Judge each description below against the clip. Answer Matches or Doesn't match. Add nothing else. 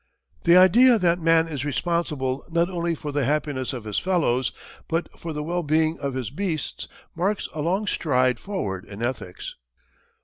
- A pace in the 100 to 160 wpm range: Doesn't match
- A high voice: Doesn't match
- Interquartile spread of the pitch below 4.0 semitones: Doesn't match